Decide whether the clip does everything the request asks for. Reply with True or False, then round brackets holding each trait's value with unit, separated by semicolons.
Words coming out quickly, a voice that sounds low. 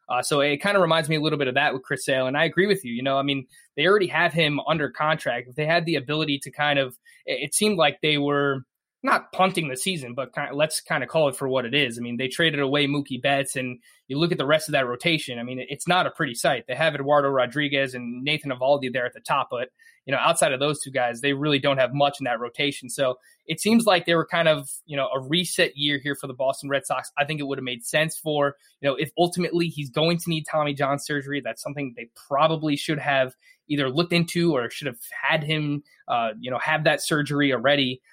False (270 wpm; 145 Hz)